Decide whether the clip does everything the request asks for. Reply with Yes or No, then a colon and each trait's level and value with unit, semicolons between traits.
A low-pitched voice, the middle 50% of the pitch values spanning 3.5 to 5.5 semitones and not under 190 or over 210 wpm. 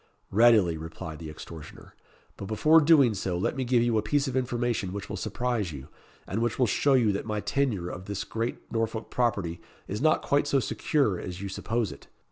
Yes: low, 110 Hz; average, 5.0 semitones; fast, 205 wpm